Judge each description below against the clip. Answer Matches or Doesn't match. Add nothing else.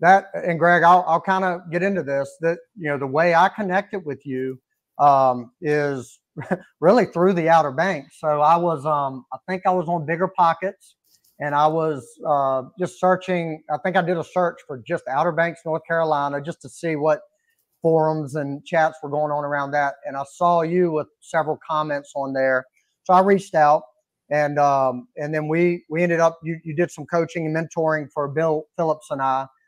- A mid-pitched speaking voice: Matches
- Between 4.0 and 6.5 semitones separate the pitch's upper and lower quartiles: Doesn't match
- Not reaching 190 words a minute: Doesn't match